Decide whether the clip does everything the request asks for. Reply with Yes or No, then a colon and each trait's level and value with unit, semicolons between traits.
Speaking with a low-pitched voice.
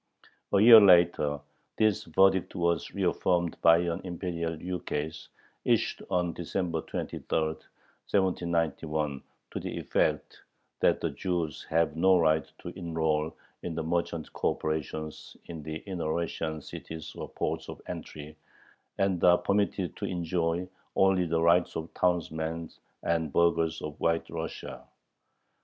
Yes: very low, 85 Hz